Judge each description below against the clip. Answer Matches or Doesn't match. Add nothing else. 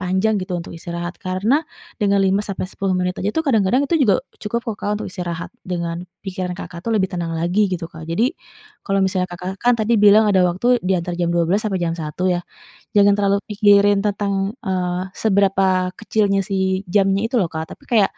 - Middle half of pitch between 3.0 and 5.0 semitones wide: Doesn't match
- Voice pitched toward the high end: Matches